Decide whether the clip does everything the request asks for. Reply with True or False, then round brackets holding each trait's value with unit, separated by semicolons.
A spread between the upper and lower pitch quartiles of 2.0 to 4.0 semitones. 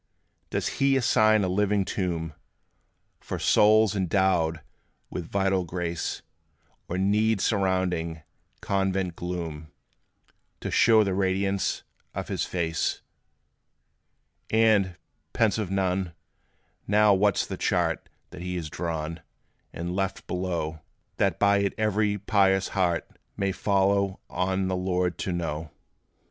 True (2.4 semitones)